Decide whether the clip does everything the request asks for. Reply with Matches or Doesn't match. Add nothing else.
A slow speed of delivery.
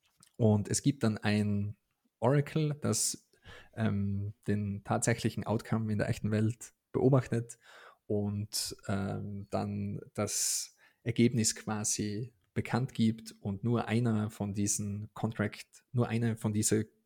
Matches